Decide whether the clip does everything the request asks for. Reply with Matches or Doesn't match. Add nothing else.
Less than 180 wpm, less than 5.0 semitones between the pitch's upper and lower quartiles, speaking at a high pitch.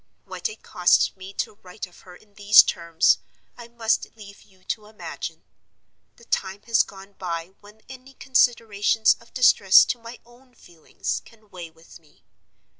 Matches